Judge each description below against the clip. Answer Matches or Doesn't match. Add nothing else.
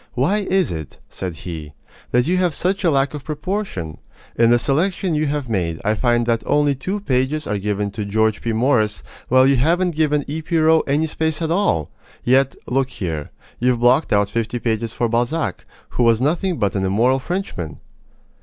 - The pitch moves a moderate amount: Doesn't match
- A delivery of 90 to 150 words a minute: Doesn't match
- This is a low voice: Matches